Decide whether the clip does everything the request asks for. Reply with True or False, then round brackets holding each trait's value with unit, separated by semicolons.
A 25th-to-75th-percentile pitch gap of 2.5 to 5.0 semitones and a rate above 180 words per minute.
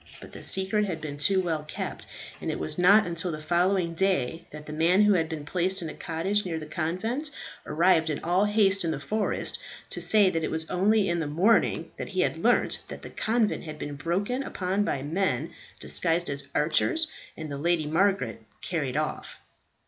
True (4.0 semitones; 200 wpm)